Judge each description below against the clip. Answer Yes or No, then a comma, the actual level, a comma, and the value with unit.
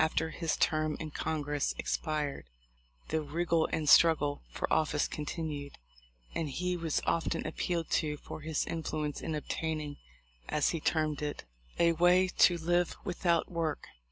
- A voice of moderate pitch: Yes, medium, 160 Hz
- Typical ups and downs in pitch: No, narrow, 2.0 semitones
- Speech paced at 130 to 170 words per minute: Yes, average, 150 wpm